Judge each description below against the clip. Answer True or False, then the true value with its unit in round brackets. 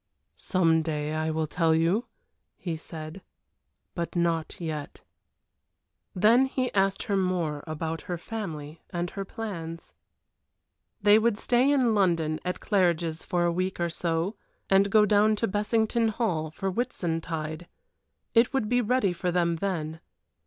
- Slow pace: False (145 wpm)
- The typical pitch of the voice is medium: True (175 Hz)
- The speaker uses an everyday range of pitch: True (4.5 semitones)